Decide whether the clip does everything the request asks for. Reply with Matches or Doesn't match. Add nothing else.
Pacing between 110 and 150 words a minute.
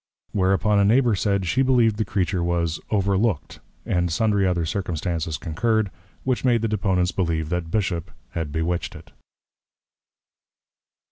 Matches